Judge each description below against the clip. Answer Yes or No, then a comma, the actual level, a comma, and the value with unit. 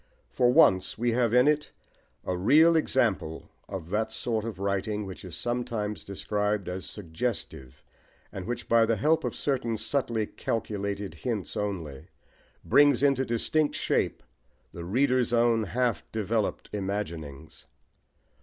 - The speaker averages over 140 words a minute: No, slow, 135 wpm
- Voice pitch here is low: Yes, low, 110 Hz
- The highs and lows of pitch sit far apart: No, average, 4.0 semitones